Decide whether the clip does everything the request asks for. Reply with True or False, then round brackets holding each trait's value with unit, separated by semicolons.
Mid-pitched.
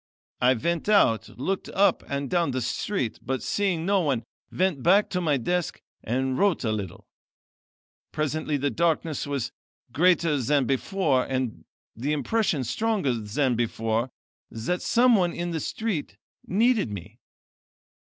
True (150 Hz)